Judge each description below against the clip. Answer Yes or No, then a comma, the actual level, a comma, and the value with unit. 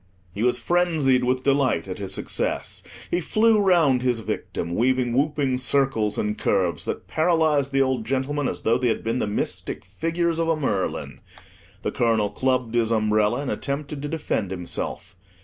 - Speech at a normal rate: Yes, average, 170 wpm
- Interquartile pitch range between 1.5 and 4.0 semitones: No, average, 5.0 semitones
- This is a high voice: No, low, 130 Hz